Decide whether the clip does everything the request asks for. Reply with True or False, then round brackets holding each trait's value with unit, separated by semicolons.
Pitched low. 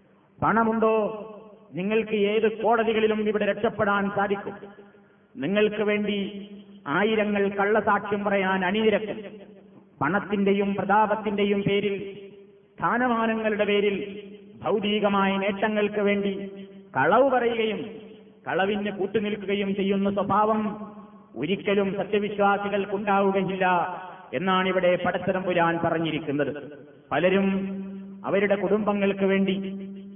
False (200 Hz)